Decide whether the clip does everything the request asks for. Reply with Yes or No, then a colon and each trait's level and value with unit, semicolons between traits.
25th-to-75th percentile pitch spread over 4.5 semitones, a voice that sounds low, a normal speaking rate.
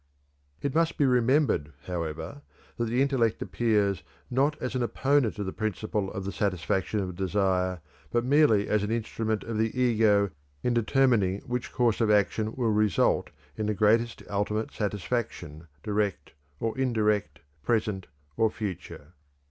No: average, 3.3 semitones; low, 110 Hz; average, 150 wpm